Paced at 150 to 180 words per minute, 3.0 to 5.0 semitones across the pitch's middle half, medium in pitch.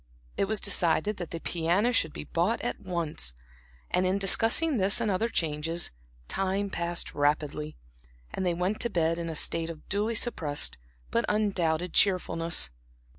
Yes: average, 160 wpm; average, 3.8 semitones; medium, 180 Hz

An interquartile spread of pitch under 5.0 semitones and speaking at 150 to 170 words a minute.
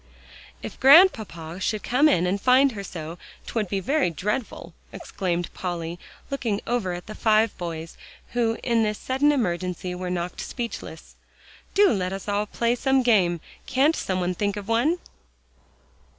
No: wide, 5.4 semitones; average, 155 wpm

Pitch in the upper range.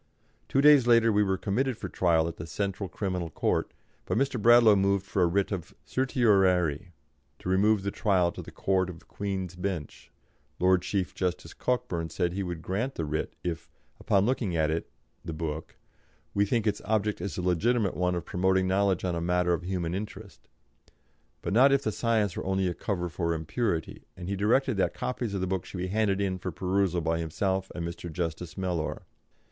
No: very low, 95 Hz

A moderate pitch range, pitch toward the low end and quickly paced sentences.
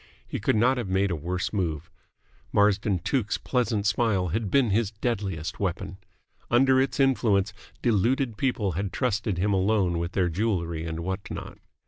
No: average, 4.1 semitones; low, 100 Hz; average, 160 wpm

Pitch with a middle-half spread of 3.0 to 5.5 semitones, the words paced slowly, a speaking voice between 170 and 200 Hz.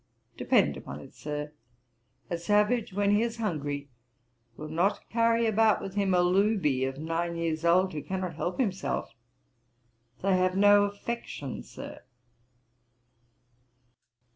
Yes: average, 4.1 semitones; slow, 130 wpm; medium, 185 Hz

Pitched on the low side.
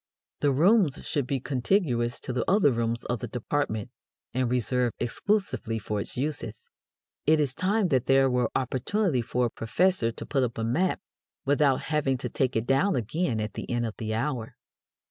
Yes: low, 130 Hz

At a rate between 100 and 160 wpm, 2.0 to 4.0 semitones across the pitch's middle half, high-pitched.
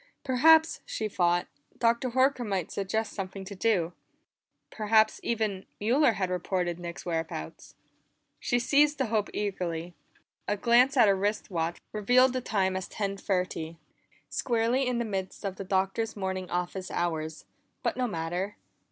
No: average, 150 wpm; average, 4.4 semitones; high, 200 Hz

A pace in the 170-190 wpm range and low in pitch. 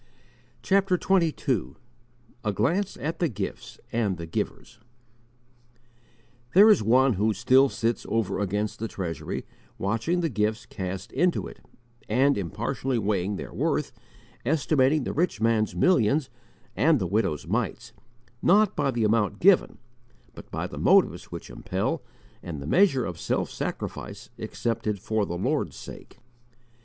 No: average, 140 wpm; low, 115 Hz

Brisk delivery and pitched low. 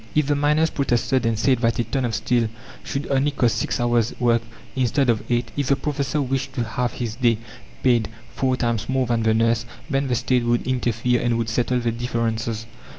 Yes: fast, 210 wpm; low, 120 Hz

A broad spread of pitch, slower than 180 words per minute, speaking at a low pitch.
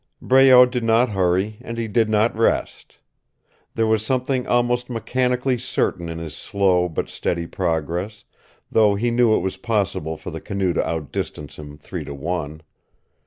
Yes: wide, 5.8 semitones; average, 165 wpm; low, 105 Hz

